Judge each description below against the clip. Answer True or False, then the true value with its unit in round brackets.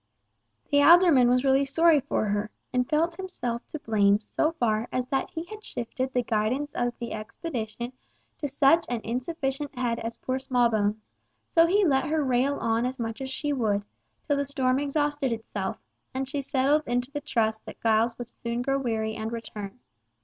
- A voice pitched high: True (255 Hz)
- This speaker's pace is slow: False (185 wpm)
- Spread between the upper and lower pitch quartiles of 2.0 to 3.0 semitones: False (4.0 semitones)